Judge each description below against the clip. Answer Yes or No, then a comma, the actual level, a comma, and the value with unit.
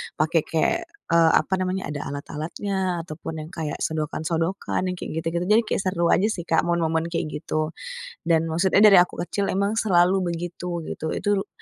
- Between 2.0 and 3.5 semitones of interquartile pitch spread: Yes, average, 2.7 semitones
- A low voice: No, medium, 170 Hz